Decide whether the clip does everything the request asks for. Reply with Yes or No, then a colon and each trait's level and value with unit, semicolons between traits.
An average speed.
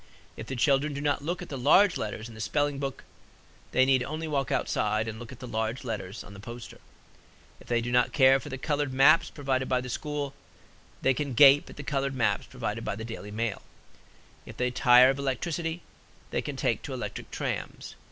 No: fast, 210 wpm